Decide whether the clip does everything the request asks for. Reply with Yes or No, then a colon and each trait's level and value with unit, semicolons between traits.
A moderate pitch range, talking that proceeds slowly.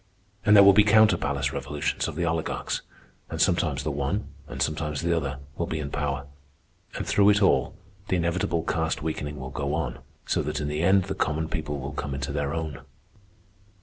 No: average, 3.1 semitones; average, 200 wpm